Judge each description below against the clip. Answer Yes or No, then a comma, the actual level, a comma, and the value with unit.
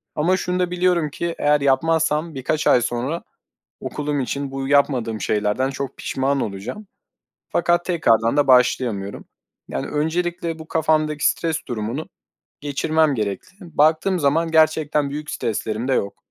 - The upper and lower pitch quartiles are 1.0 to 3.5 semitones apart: No, average, 4.0 semitones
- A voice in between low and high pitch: Yes, medium, 145 Hz